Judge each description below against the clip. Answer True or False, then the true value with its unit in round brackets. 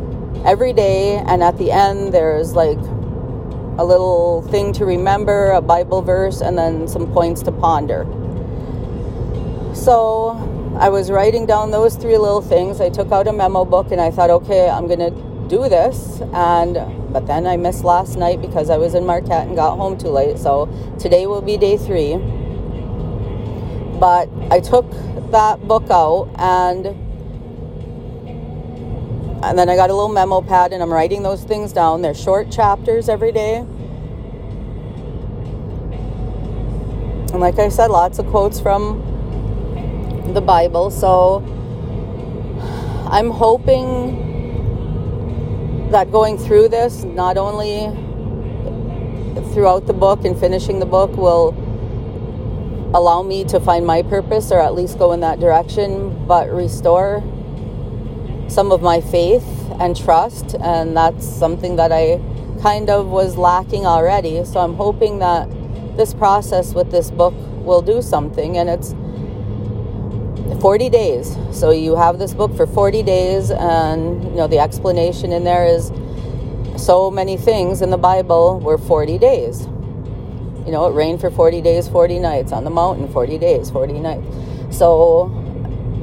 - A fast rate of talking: False (145 wpm)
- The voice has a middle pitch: True (175 Hz)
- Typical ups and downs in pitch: False (7.5 semitones)